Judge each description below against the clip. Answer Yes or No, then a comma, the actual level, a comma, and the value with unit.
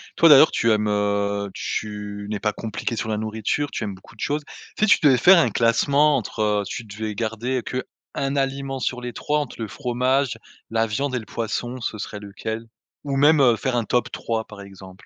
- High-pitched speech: No, low, 115 Hz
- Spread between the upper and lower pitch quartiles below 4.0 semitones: No, average, 4.3 semitones